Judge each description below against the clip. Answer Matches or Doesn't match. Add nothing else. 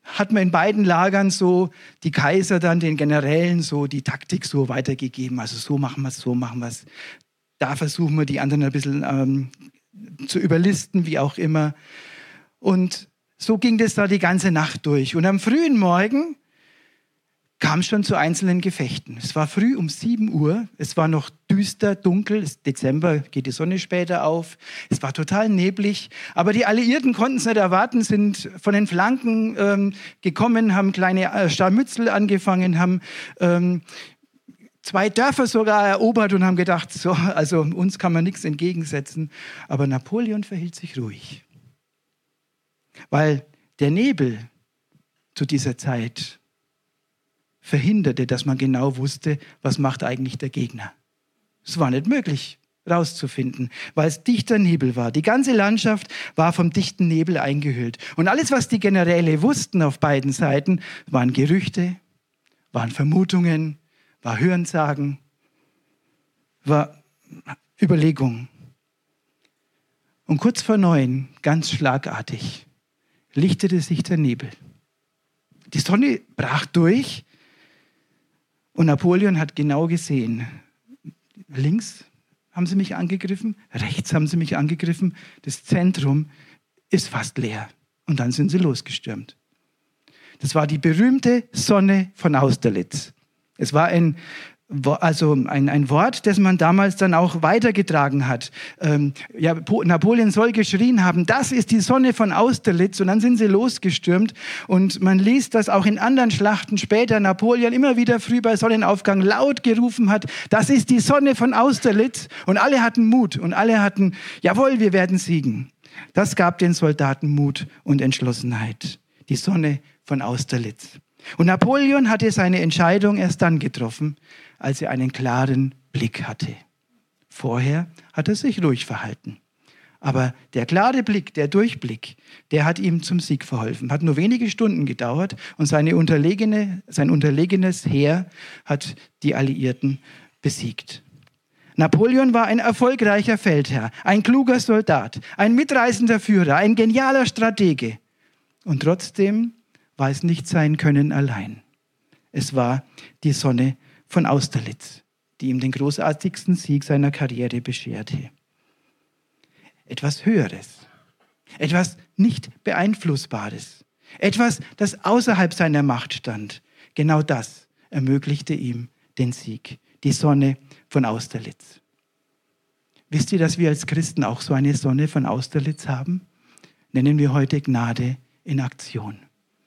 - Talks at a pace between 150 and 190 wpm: Doesn't match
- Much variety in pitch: Matches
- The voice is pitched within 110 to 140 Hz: Doesn't match